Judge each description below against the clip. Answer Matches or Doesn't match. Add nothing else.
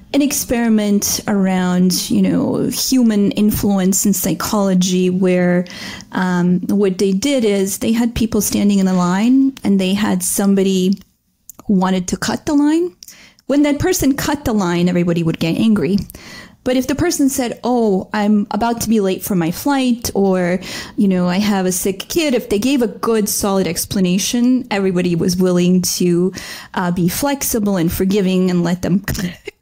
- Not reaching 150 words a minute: Doesn't match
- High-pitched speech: Matches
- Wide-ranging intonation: Doesn't match